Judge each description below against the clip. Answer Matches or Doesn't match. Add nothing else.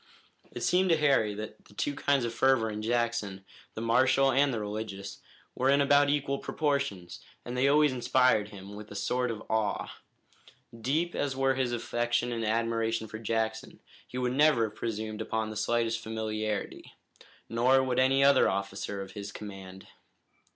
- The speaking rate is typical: Matches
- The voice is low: Matches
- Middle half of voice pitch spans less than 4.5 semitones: Matches